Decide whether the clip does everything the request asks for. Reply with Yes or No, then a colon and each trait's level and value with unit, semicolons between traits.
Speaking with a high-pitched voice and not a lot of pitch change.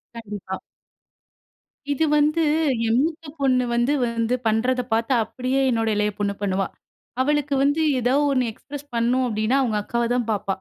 No: high, 240 Hz; average, 3.5 semitones